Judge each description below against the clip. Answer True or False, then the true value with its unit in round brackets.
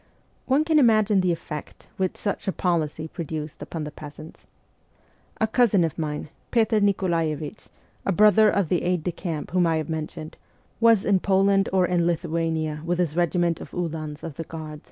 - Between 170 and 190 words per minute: True (175 wpm)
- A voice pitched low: False (170 Hz)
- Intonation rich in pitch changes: False (3.8 semitones)